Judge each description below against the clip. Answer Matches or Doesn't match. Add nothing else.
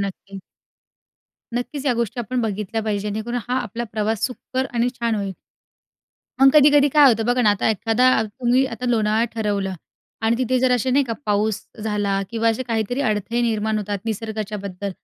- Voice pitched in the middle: Doesn't match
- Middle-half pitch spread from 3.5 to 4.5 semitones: Doesn't match